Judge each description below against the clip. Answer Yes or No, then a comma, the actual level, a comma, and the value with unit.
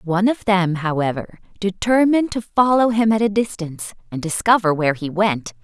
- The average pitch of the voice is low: No, high, 195 Hz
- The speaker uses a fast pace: No, average, 170 wpm